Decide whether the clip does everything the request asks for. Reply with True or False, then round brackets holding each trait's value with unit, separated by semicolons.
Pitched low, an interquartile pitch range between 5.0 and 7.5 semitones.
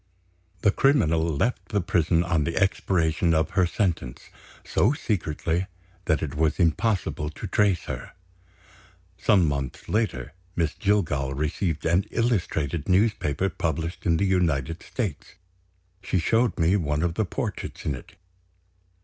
False (85 Hz; 3.9 semitones)